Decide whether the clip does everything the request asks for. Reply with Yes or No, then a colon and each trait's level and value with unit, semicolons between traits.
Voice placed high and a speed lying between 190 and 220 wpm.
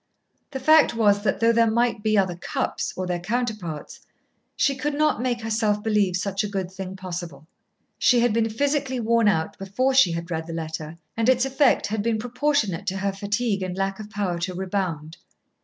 Yes: high, 210 Hz; average, 195 wpm